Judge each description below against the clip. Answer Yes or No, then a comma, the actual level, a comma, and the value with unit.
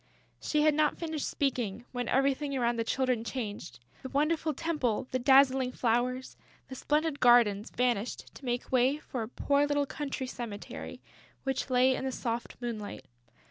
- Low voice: No, very high, 255 Hz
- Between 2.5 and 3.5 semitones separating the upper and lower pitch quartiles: Yes, average, 2.8 semitones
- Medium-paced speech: Yes, average, 160 wpm